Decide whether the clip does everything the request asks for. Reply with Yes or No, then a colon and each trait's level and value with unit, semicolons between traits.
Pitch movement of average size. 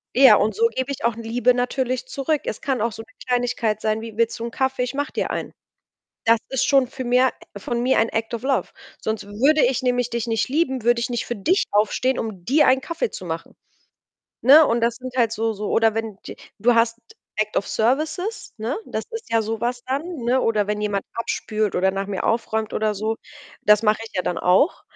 Yes: average, 3.1 semitones